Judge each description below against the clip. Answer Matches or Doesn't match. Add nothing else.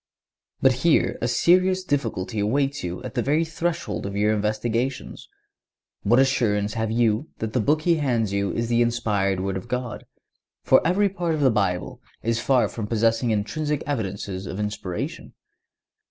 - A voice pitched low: Matches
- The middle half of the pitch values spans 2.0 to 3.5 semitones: Doesn't match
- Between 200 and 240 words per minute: Doesn't match